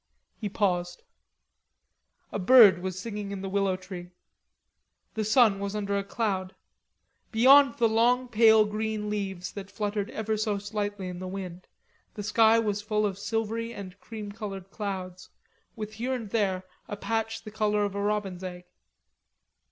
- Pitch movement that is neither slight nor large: No, narrow, 2.3 semitones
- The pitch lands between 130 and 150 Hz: No, high, 205 Hz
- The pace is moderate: Yes, average, 160 wpm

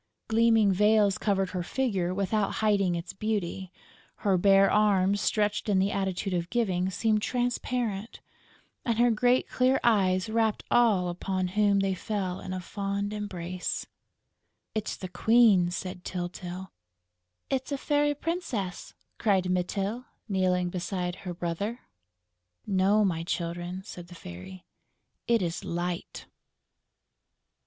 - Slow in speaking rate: Yes, slow, 130 wpm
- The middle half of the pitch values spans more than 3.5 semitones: No, average, 3.1 semitones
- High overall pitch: Yes, high, 195 Hz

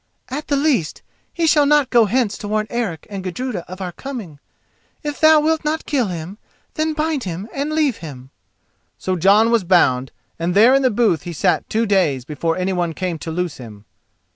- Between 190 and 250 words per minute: Yes, average, 195 wpm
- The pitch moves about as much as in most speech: No, wide, 8.1 semitones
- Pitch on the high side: Yes, high, 205 Hz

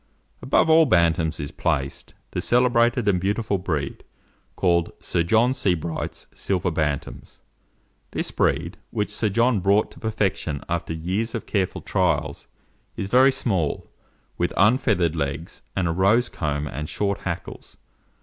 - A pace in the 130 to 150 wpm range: Yes, average, 140 wpm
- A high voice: No, very low, 95 Hz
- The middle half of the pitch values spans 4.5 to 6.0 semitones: Yes, average, 5.2 semitones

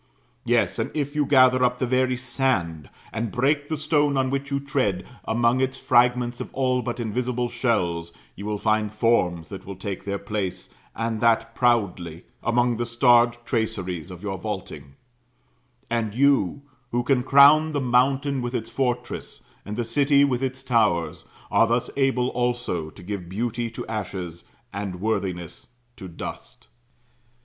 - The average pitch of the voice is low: Yes, low, 120 Hz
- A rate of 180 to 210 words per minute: No, average, 160 wpm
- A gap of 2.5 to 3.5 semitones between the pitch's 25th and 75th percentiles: No, average, 4.3 semitones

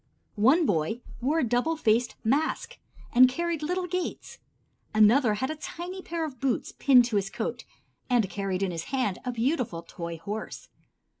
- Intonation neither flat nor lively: No, wide, 7.0 semitones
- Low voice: No, very high, 250 Hz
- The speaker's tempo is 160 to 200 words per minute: Yes, average, 165 wpm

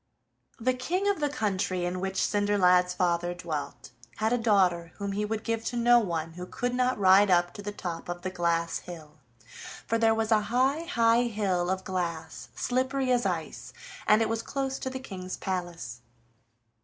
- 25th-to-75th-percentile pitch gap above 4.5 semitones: Yes, average, 5.0 semitones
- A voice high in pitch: Yes, high, 200 Hz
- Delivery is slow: No, average, 185 wpm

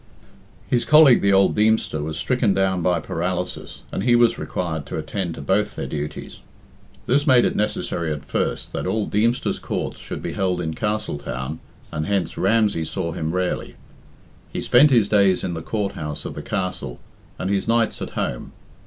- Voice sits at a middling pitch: No, very low, 95 Hz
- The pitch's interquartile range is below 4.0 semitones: No, average, 5.0 semitones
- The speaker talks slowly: No, average, 180 wpm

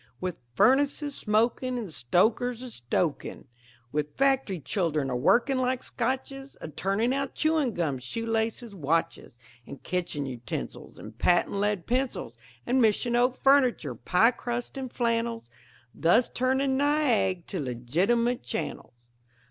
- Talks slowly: Yes, slow, 130 wpm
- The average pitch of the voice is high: Yes, high, 230 Hz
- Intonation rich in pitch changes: Yes, wide, 7.4 semitones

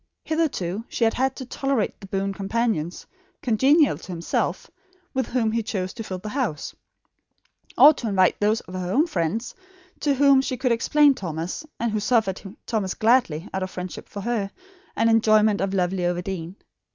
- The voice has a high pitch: Yes, high, 215 Hz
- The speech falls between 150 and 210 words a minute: Yes, average, 175 wpm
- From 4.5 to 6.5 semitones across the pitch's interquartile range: Yes, average, 5.1 semitones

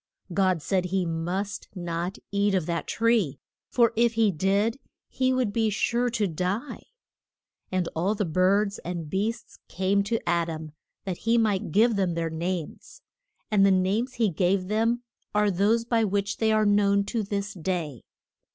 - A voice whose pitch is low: No, high, 200 Hz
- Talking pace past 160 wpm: Yes, average, 170 wpm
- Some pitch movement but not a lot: Yes, average, 3.4 semitones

